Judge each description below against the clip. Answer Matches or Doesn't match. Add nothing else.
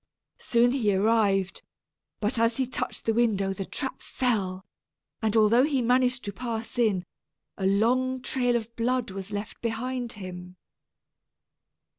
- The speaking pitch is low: Doesn't match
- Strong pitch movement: Doesn't match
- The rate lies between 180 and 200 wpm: Doesn't match